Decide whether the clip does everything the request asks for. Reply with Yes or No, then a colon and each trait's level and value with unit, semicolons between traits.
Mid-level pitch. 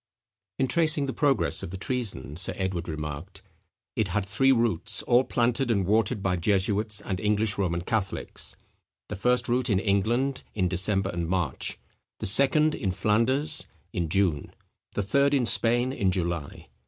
No: low, 105 Hz